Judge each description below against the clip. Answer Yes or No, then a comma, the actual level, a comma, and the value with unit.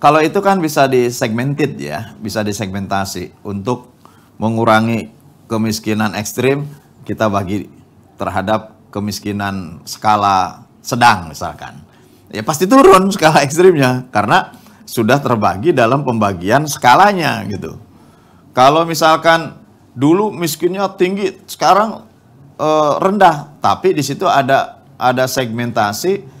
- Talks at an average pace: Yes, average, 100 wpm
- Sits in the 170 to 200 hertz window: No, low, 130 Hz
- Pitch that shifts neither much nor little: No, wide, 6.7 semitones